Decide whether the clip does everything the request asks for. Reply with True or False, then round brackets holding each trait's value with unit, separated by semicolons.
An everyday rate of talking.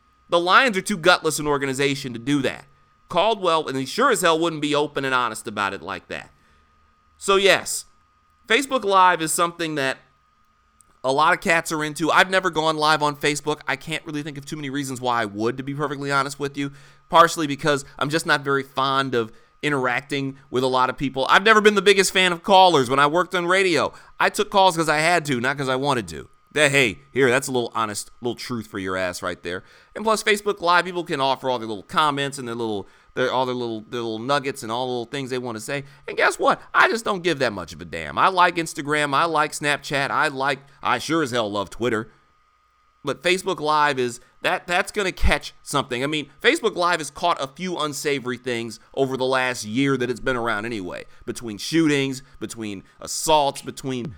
False (225 wpm)